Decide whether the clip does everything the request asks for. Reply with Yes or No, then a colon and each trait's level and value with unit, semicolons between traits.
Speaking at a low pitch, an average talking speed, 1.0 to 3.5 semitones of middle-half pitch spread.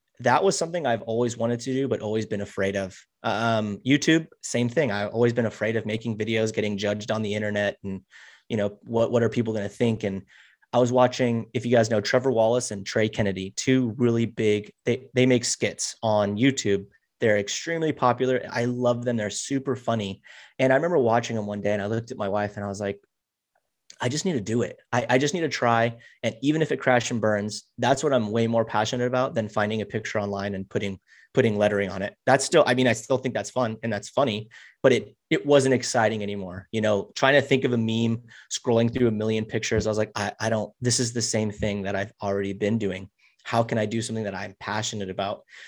No: low, 115 Hz; fast, 235 wpm; average, 2.9 semitones